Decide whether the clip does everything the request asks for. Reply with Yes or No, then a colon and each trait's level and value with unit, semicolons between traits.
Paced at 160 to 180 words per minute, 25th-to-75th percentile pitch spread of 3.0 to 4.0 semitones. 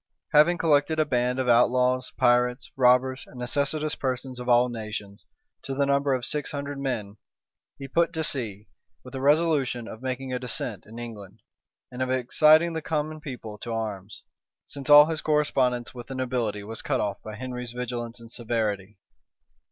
Yes: average, 175 wpm; average, 3.3 semitones